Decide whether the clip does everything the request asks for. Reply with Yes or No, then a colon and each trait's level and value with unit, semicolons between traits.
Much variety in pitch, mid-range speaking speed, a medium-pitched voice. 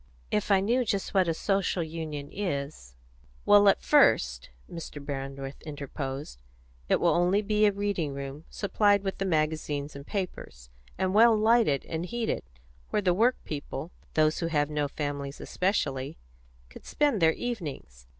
Yes: wide, 6.1 semitones; average, 160 wpm; medium, 160 Hz